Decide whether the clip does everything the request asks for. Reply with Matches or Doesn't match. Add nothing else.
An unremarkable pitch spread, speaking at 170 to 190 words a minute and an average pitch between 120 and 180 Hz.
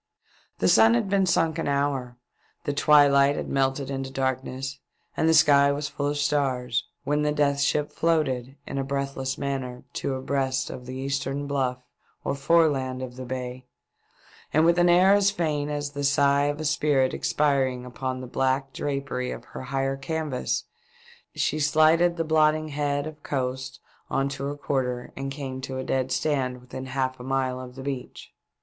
Doesn't match